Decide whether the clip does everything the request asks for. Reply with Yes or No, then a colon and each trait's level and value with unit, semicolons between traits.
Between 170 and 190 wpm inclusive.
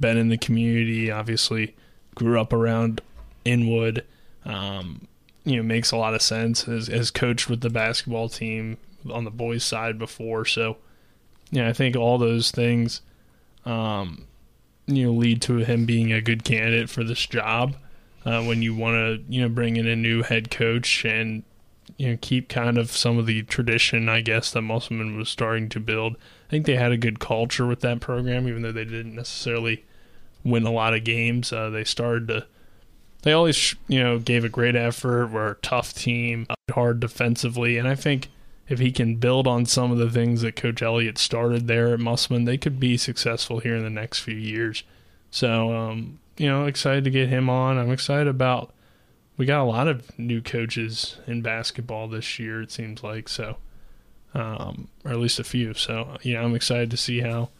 No: average, 200 wpm